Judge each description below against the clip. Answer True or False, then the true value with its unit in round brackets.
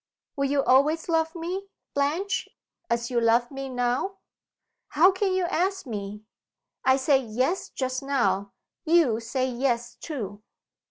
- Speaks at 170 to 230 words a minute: False (140 wpm)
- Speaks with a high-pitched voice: True (270 Hz)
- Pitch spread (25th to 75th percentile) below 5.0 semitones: False (5.5 semitones)